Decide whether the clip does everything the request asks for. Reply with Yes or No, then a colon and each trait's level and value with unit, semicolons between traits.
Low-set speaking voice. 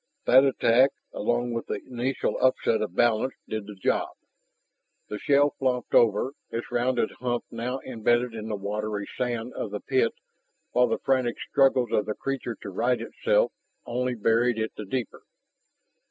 Yes: low, 120 Hz